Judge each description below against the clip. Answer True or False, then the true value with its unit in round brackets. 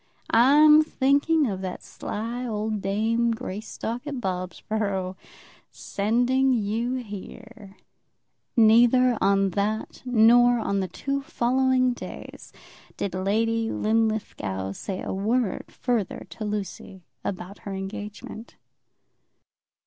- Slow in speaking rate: True (105 wpm)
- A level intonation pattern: False (3.6 semitones)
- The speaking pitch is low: False (220 Hz)